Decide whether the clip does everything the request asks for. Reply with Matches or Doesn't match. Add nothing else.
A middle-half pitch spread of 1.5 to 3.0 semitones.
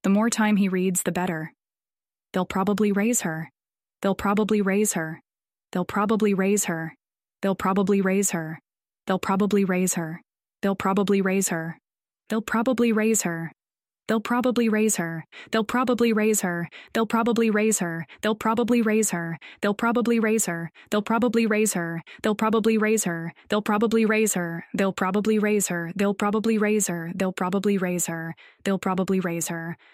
Doesn't match